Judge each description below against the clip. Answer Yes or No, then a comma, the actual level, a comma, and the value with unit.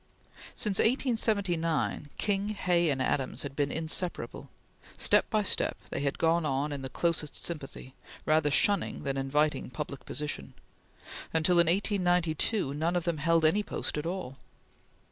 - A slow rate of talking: No, average, 145 wpm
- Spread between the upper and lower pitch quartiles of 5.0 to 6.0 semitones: No, average, 3.7 semitones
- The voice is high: No, medium, 160 Hz